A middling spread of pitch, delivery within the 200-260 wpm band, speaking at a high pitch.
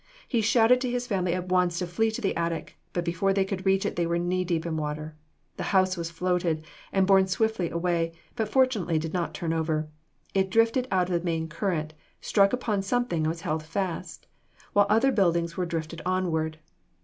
No: average, 3.1 semitones; fast, 205 wpm; medium, 180 Hz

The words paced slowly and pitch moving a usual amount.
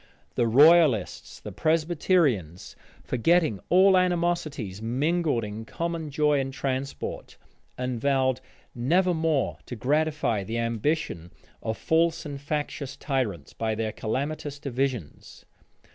No: slow, 115 wpm; wide, 5.7 semitones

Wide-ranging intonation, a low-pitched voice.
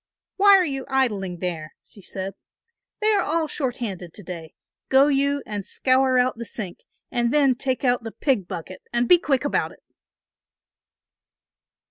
No: wide, 6.0 semitones; very high, 250 Hz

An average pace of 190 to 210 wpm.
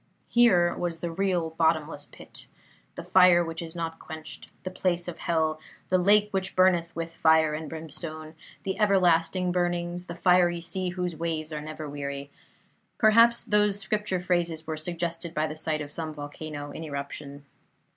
No: average, 165 wpm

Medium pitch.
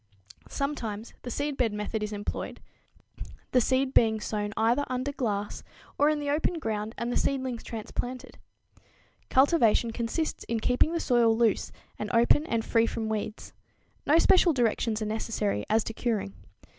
No: high, 235 Hz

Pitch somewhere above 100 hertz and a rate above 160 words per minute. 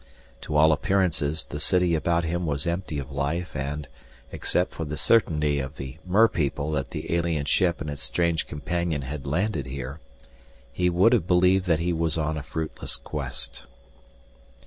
No: very low, 80 Hz; average, 170 wpm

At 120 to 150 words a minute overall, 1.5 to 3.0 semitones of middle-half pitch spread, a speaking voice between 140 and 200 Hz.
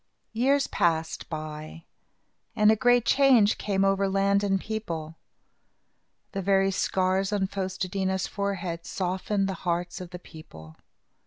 Yes: average, 145 wpm; narrow, 2.5 semitones; high, 190 Hz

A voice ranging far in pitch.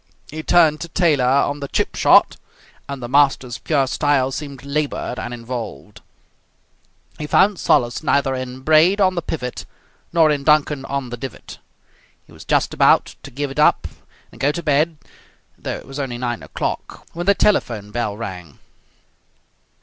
No: average, 3.6 semitones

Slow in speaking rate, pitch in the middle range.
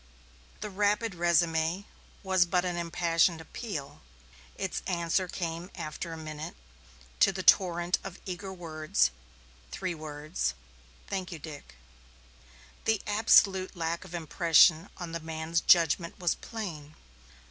Yes: slow, 125 wpm; medium, 170 Hz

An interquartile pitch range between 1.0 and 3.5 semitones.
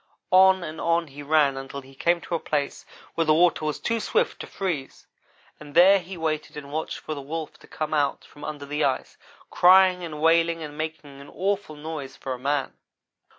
Yes: average, 2.9 semitones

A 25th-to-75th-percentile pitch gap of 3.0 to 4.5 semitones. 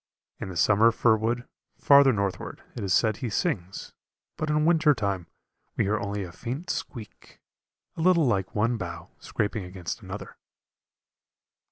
No: wide, 5.5 semitones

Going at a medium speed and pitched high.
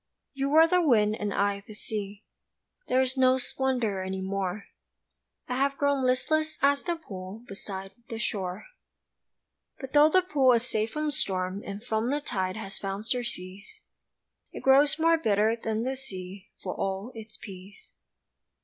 Yes: average, 160 wpm; high, 225 Hz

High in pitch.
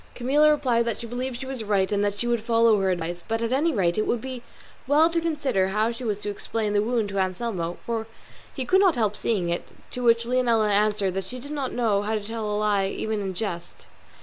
Yes: high, 225 Hz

